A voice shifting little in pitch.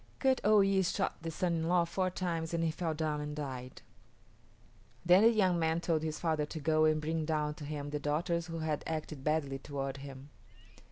Yes: narrow, 2.3 semitones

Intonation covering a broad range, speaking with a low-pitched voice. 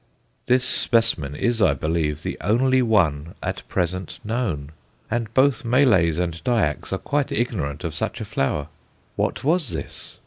Yes: wide, 7.6 semitones; low, 100 Hz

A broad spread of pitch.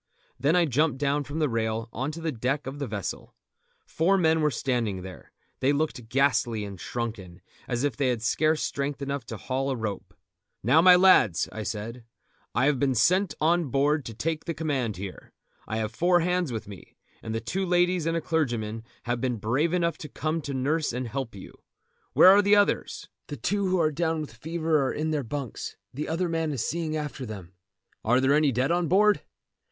Yes: wide, 5.7 semitones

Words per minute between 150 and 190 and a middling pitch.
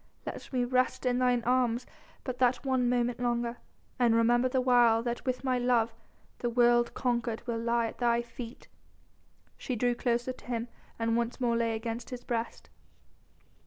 No: average, 170 wpm; high, 240 Hz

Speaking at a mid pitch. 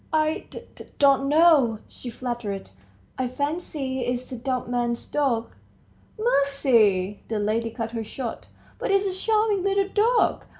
No: very high, 260 Hz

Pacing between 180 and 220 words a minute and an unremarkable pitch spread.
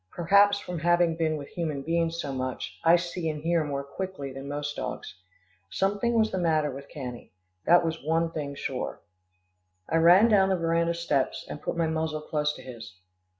Yes: average, 190 wpm; average, 3.0 semitones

